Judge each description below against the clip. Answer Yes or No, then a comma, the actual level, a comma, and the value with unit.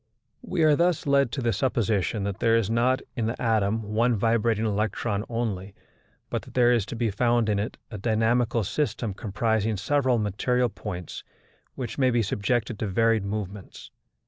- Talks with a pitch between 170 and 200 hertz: No, low, 115 Hz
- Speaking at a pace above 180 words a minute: No, average, 170 wpm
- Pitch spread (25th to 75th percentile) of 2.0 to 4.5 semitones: Yes, average, 2.7 semitones